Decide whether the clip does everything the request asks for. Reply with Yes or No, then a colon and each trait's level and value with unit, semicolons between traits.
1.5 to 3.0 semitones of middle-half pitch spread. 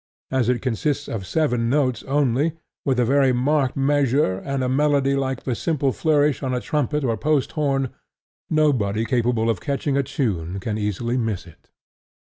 No: average, 3.6 semitones